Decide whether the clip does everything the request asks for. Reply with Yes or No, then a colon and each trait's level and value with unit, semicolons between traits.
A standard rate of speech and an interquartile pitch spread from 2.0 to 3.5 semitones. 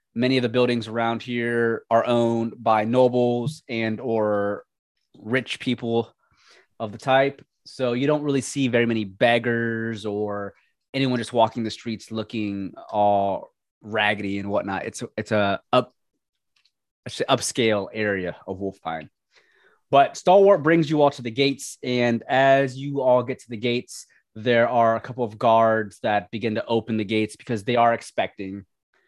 Yes: average, 165 wpm; average, 2.7 semitones